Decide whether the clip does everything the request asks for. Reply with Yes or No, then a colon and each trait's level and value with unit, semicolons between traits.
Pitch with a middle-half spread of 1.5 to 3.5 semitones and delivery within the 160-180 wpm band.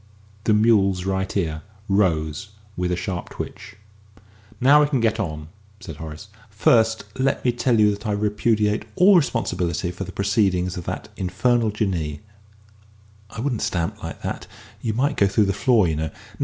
No: average, 4.0 semitones; average, 170 wpm